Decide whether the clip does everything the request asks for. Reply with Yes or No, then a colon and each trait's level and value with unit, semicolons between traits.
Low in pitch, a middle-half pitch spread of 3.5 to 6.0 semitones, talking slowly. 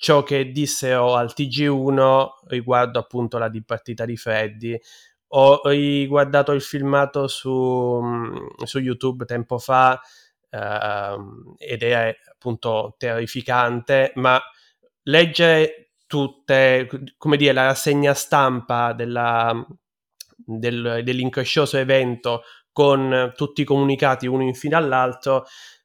No: low, 130 Hz; average, 2.7 semitones; slow, 105 wpm